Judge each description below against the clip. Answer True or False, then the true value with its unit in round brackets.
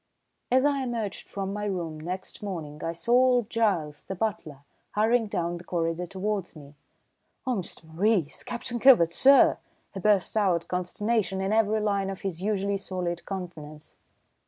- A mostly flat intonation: False (4.2 semitones)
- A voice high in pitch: True (195 Hz)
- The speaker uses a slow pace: False (160 wpm)